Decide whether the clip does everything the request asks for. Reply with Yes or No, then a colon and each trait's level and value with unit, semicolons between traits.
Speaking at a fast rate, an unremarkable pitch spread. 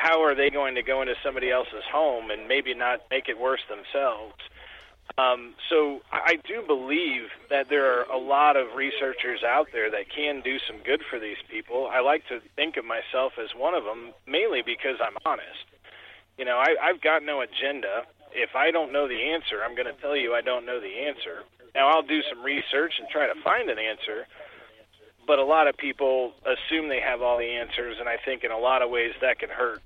Yes: fast, 220 wpm; average, 4.2 semitones